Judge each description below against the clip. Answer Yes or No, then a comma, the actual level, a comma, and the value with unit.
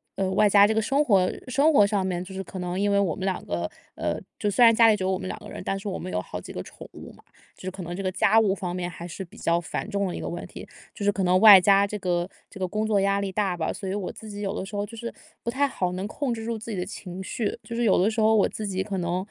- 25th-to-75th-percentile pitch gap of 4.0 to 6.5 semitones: No, narrow, 2.6 semitones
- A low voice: No, high, 195 Hz